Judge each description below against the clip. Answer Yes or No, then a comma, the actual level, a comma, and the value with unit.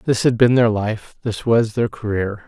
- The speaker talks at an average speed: No, fast, 220 wpm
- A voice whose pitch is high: No, low, 110 Hz